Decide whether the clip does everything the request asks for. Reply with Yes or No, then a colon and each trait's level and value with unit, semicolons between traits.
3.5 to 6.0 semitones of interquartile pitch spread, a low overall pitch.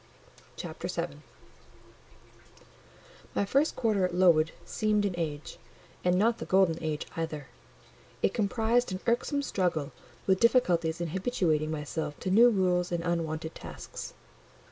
No: average, 4.8 semitones; medium, 180 Hz